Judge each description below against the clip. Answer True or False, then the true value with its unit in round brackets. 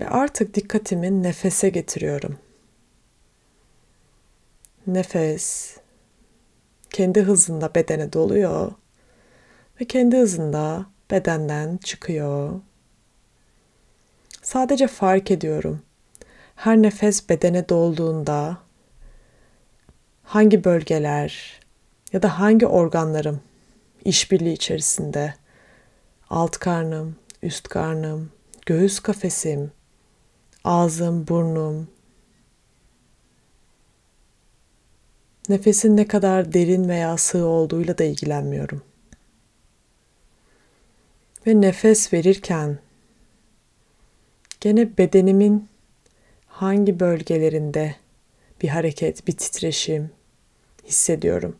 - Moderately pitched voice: True (175 Hz)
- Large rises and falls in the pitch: False (4.0 semitones)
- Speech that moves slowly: True (70 wpm)